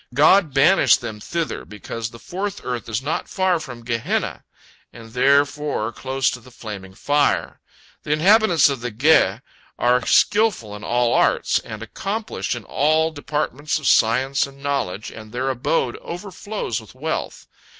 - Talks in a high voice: No, low, 135 Hz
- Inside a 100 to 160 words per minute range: Yes, average, 150 wpm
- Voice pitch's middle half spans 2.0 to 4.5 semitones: No, average, 5.2 semitones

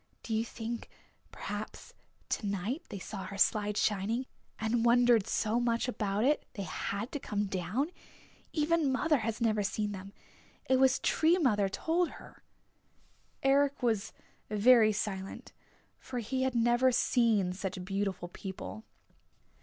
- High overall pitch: Yes, high, 225 Hz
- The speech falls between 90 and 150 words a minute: Yes, average, 140 wpm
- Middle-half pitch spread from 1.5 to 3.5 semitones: No, average, 4.0 semitones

